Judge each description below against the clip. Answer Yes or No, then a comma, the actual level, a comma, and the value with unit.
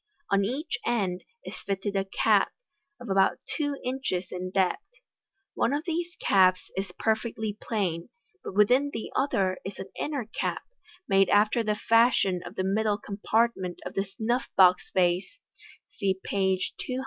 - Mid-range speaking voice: No, high, 205 Hz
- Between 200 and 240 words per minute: No, average, 160 wpm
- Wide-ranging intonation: No, average, 3.7 semitones